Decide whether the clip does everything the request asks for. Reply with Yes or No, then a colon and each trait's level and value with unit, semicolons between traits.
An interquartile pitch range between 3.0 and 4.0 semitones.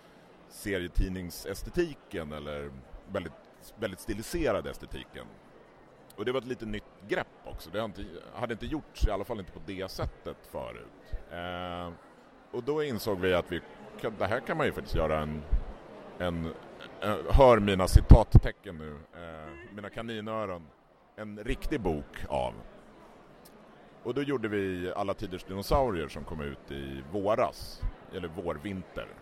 No: average, 5.0 semitones